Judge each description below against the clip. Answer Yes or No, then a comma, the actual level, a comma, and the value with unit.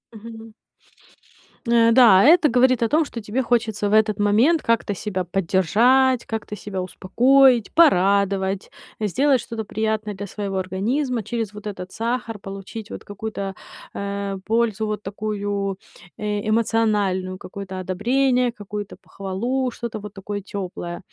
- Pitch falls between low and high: No, high, 210 Hz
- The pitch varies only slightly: No, average, 3.0 semitones